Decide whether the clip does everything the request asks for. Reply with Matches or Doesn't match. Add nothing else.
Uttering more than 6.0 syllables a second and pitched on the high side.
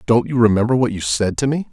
Doesn't match